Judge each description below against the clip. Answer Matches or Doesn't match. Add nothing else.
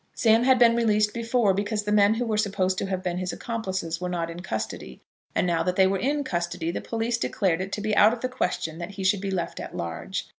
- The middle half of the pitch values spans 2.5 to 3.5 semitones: Doesn't match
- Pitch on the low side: Doesn't match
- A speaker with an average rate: Doesn't match